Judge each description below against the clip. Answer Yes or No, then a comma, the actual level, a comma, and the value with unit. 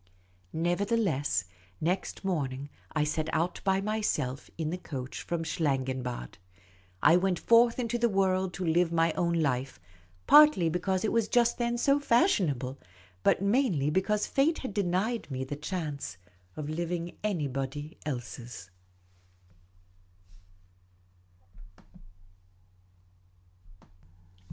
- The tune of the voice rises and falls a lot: Yes, wide, 6.3 semitones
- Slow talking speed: Yes, slow, 115 wpm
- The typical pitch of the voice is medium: Yes, medium, 170 Hz